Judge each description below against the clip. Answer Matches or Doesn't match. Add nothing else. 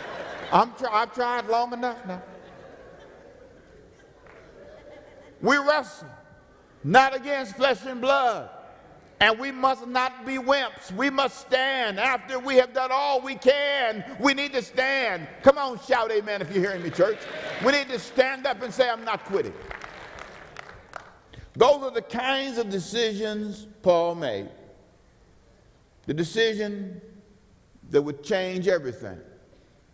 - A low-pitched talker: Doesn't match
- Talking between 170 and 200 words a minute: Doesn't match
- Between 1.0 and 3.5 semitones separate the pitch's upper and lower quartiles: Doesn't match